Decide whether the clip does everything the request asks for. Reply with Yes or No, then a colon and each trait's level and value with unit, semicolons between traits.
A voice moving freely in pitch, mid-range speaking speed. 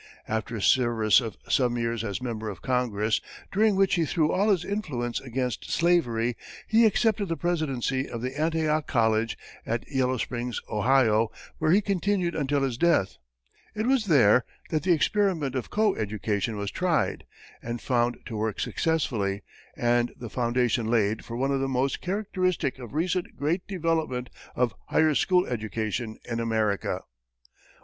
Yes: wide, 6.4 semitones; average, 155 wpm